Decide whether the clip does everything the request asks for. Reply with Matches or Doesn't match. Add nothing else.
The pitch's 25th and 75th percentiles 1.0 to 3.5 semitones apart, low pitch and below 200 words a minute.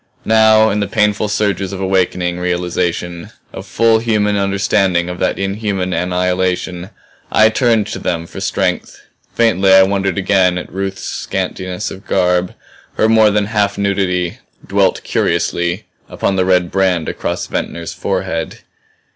Matches